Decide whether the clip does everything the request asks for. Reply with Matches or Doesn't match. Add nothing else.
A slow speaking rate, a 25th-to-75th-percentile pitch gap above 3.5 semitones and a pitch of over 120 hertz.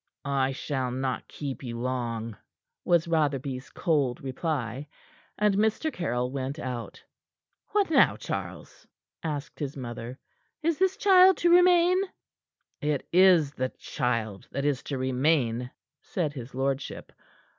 Matches